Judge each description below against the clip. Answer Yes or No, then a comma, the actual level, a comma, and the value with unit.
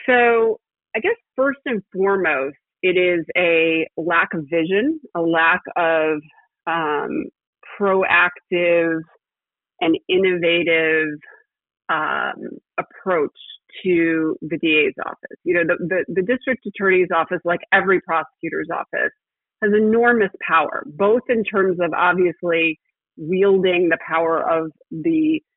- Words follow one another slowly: Yes, slow, 115 wpm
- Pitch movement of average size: Yes, average, 4.6 semitones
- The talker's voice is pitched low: No, medium, 180 Hz